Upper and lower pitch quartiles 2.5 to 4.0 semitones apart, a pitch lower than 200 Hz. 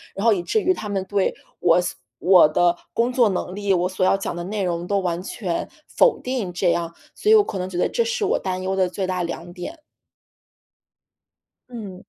Yes: average, 3.5 semitones; high, 190 Hz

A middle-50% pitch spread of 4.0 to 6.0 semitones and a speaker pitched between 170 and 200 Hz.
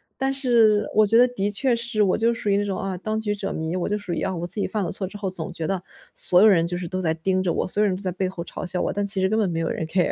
No: average, 2.9 semitones; high, 195 Hz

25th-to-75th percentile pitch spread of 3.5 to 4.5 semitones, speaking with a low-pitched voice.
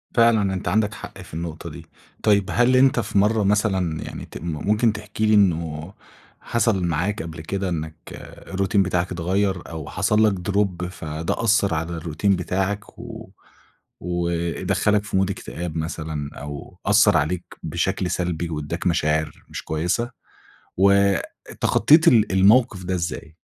Yes: average, 3.8 semitones; very low, 95 Hz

